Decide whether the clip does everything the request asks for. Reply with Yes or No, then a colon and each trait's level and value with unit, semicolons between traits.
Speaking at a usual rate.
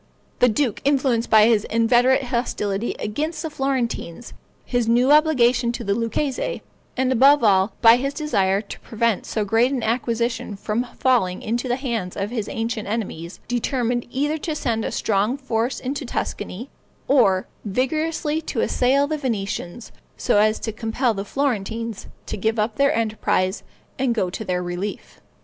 Yes: average, 160 wpm